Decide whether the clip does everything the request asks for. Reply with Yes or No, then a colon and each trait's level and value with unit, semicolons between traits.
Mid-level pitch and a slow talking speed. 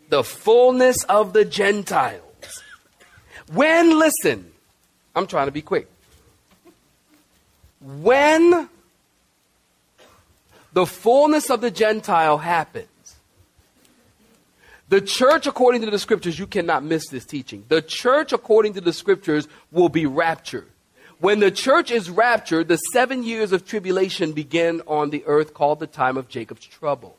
Yes: medium, 180 Hz; slow, 130 wpm